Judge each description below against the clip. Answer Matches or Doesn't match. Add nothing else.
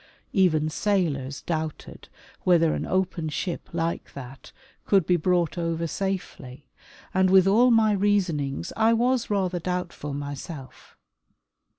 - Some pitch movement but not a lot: Matches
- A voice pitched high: Doesn't match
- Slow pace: Matches